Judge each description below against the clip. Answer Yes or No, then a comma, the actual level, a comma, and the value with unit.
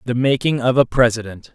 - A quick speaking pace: No, average, 195 wpm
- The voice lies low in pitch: Yes, low, 125 Hz